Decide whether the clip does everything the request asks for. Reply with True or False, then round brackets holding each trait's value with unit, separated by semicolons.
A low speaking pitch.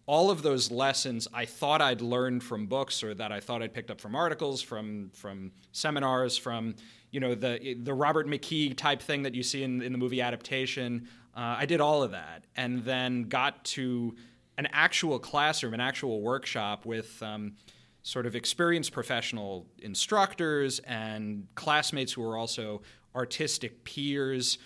True (125 Hz)